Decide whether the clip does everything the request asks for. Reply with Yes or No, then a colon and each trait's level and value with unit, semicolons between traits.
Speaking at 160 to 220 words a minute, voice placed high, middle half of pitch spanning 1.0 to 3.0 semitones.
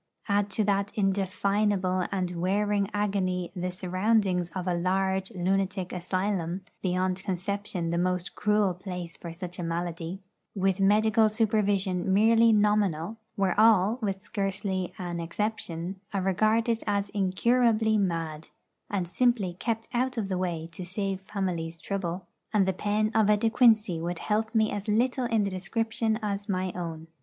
No: average, 150 wpm; high, 195 Hz; average, 2.7 semitones